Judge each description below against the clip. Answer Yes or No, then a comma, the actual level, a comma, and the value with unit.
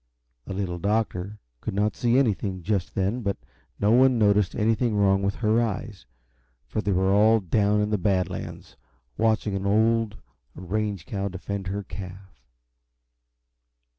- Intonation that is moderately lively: No, narrow, 2.1 semitones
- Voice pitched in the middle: No, low, 100 Hz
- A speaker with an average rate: Yes, average, 150 wpm